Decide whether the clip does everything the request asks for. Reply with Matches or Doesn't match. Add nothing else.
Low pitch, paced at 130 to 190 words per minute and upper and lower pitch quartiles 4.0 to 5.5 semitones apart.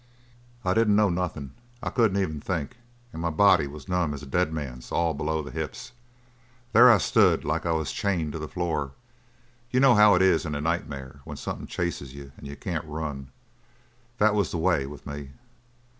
Doesn't match